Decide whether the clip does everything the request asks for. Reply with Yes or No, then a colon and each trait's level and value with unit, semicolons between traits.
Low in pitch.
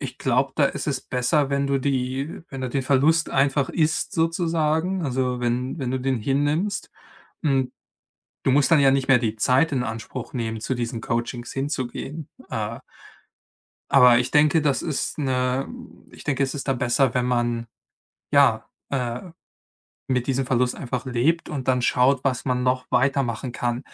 Yes: low, 130 Hz